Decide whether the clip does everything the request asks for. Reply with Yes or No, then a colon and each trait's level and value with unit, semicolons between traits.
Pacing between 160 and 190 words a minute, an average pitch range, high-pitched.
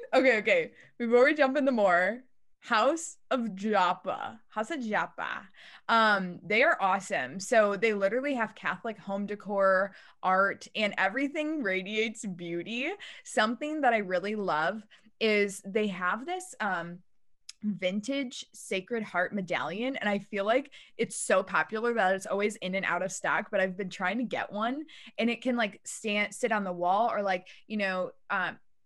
Yes: average, 165 wpm; average, 3.8 semitones; high, 210 Hz